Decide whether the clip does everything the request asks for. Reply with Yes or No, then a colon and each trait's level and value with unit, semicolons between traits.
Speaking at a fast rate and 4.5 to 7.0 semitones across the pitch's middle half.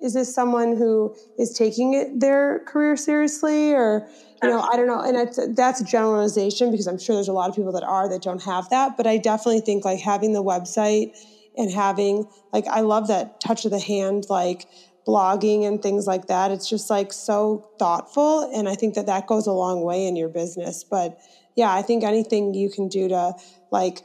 No: fast, 215 wpm; average, 3.5 semitones